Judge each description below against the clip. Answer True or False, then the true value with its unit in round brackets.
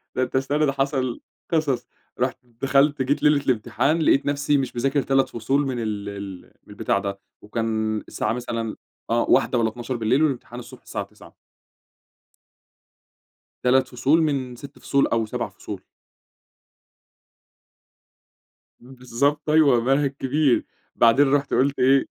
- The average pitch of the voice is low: True (130 Hz)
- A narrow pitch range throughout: False (3.2 semitones)